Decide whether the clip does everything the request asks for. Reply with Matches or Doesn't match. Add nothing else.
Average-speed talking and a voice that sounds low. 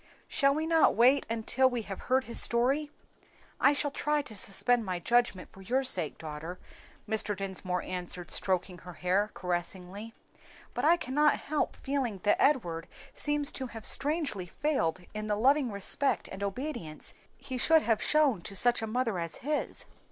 Doesn't match